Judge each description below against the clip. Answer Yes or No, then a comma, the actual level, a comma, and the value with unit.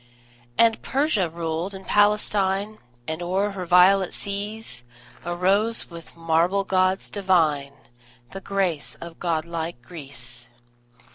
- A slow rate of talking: Yes, slow, 115 wpm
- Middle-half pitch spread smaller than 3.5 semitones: Yes, average, 3.1 semitones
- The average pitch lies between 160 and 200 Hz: Yes, medium, 185 Hz